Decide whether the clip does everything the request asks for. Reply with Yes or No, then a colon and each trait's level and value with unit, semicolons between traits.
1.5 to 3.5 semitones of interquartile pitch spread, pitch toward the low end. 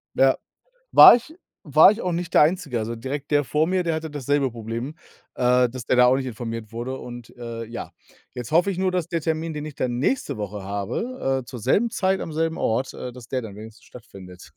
No: wide, 5.6 semitones; low, 130 Hz